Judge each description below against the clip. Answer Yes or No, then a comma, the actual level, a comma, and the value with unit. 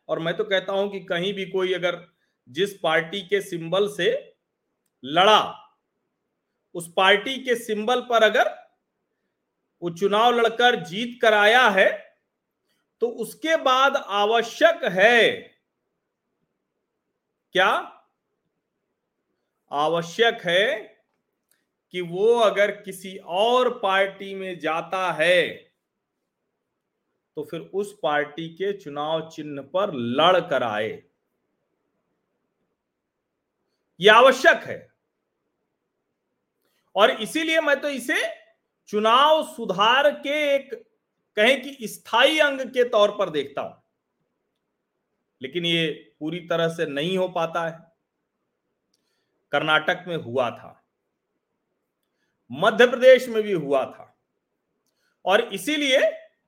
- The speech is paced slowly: Yes, slow, 105 wpm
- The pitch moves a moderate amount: No, wide, 6.7 semitones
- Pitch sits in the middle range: No, high, 200 Hz